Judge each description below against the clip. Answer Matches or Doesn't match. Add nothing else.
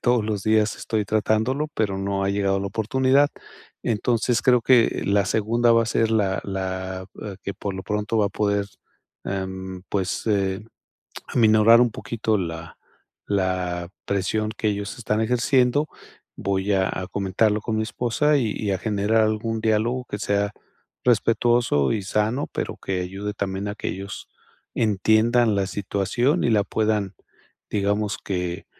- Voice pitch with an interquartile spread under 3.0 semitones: Matches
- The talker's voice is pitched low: Matches